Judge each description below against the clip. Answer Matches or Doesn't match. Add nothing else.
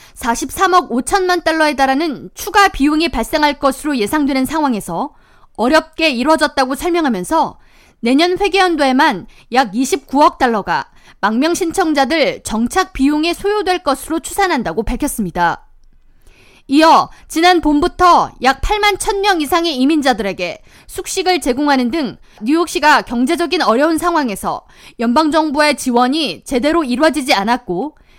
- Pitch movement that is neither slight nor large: Matches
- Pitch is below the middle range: Doesn't match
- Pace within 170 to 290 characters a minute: Doesn't match